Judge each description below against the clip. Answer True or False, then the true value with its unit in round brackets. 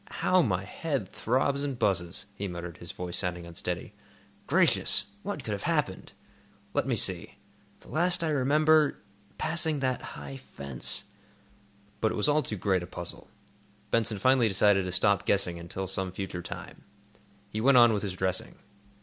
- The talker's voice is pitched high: False (100 Hz)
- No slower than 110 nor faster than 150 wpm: False (160 wpm)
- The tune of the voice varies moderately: False (6.8 semitones)